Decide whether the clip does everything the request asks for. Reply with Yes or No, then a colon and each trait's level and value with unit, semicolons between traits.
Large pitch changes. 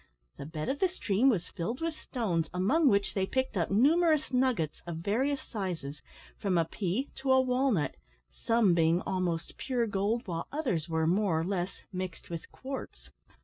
Yes: wide, 7.3 semitones